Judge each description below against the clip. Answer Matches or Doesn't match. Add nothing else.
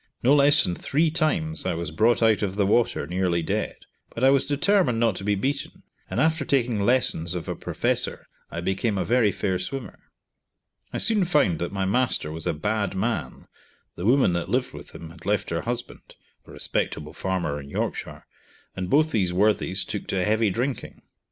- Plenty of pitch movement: Matches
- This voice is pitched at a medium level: Doesn't match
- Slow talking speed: Doesn't match